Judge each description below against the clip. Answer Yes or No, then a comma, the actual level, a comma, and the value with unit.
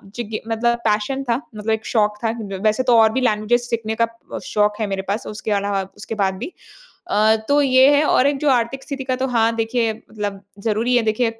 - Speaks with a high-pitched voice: Yes, high, 225 Hz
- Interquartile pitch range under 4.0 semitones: Yes, average, 2.8 semitones